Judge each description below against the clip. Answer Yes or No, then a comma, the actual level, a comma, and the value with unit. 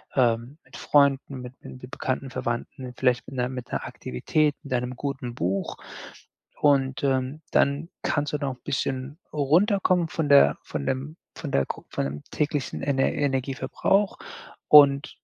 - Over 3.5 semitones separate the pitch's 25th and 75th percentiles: No, narrow, 2.5 semitones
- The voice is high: No, low, 135 Hz